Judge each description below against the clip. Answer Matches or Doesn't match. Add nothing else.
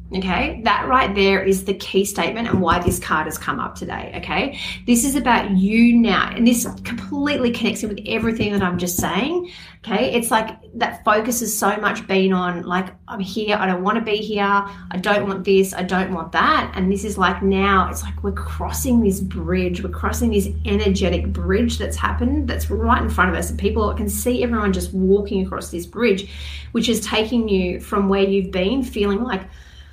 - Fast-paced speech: Matches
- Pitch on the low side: Doesn't match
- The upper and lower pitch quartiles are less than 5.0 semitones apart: Matches